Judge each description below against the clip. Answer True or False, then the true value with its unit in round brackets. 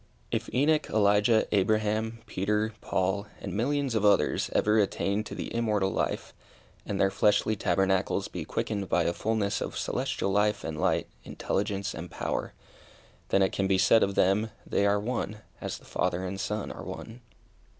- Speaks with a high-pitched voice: False (105 Hz)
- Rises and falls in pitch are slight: True (2.1 semitones)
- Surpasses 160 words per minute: True (170 wpm)